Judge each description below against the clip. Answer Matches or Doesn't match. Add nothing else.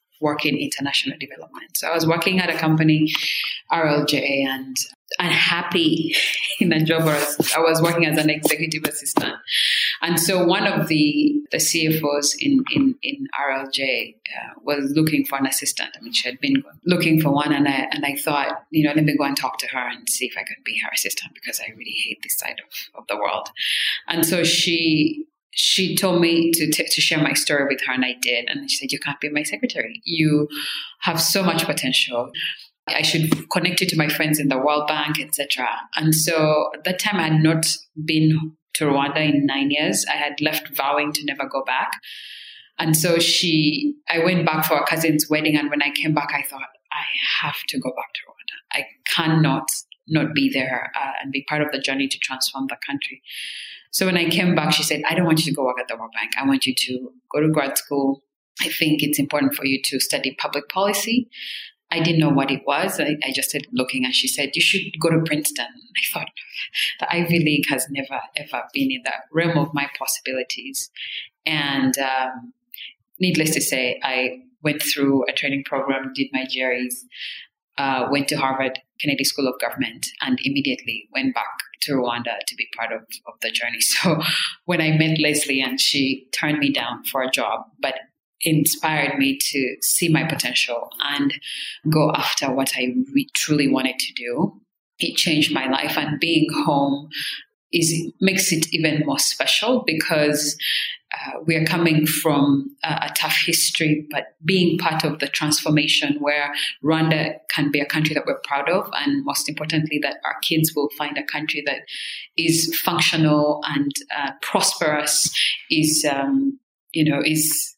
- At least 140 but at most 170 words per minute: Doesn't match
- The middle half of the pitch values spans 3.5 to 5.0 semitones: Doesn't match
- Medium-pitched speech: Matches